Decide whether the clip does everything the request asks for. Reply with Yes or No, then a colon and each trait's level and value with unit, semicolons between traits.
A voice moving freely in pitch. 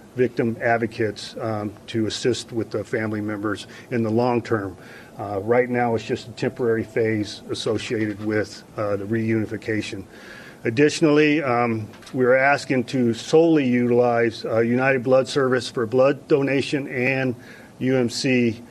No: average, 2.7 semitones